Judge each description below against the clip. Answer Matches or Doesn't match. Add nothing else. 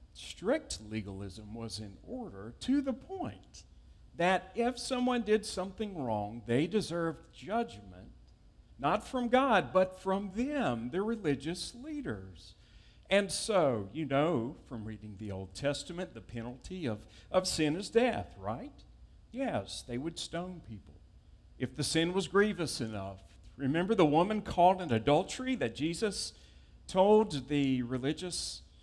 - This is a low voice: Doesn't match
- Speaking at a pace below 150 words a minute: Matches